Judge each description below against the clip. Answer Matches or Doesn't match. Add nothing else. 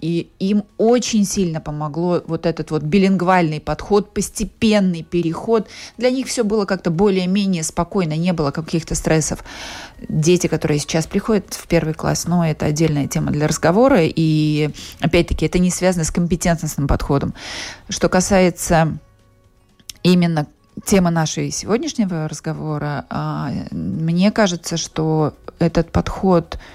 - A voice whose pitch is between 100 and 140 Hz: Doesn't match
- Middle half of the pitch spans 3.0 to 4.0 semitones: Matches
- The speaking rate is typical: Matches